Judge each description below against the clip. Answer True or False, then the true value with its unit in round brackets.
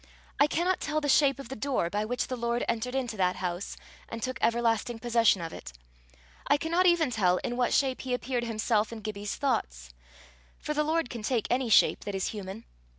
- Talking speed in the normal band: False (210 wpm)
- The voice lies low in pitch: False (235 Hz)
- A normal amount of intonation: True (4.1 semitones)